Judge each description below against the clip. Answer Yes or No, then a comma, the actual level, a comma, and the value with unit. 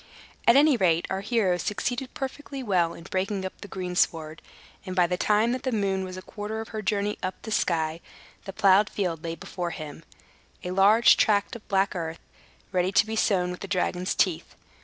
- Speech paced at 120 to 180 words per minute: No, average, 200 wpm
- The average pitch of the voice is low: No, high, 190 Hz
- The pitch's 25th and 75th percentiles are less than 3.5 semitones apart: Yes, average, 3.0 semitones